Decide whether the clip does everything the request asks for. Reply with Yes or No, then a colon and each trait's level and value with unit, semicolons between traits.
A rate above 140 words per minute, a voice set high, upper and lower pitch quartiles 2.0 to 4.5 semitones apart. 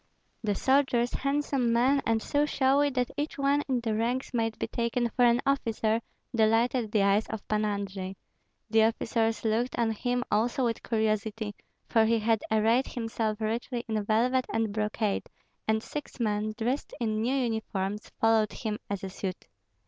Yes: average, 165 wpm; high, 225 Hz; narrow, 2.4 semitones